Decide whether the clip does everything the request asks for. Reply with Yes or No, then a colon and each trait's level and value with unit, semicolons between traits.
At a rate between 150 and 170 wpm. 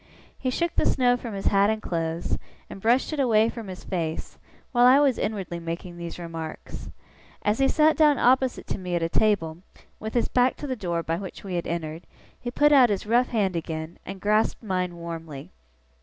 No: fast, 205 wpm